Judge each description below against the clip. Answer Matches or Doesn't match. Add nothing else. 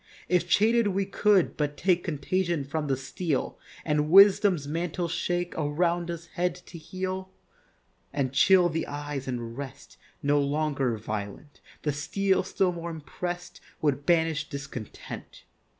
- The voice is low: Doesn't match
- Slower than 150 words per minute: Matches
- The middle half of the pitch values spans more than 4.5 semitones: Doesn't match